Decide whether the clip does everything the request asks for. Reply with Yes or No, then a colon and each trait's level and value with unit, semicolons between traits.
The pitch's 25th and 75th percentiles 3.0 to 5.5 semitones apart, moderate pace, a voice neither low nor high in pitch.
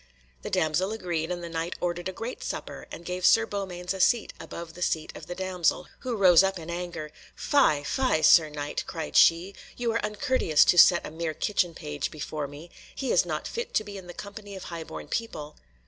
No: average, 3.8 semitones; fast, 210 wpm; medium, 175 Hz